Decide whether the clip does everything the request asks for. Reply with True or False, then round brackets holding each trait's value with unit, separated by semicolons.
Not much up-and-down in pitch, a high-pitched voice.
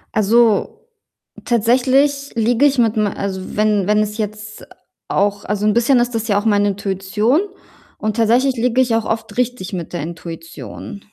False (3.0 semitones; 215 Hz)